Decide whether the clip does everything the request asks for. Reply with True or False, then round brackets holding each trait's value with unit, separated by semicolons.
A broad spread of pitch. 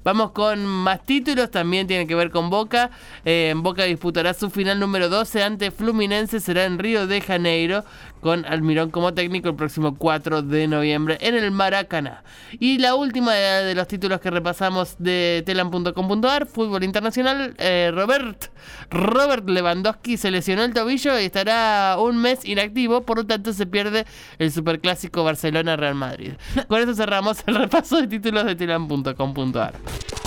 False (4.5 semitones)